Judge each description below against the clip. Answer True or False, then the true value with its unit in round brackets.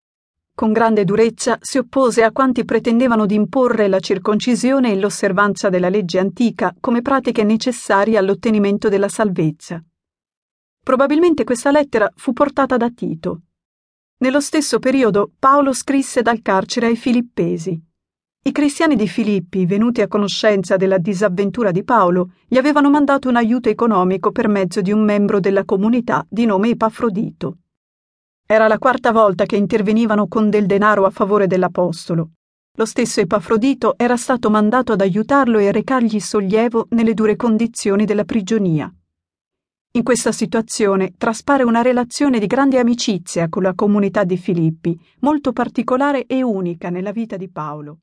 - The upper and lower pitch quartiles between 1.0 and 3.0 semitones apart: False (3.5 semitones)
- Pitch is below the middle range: False (220 Hz)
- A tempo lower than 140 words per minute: False (145 wpm)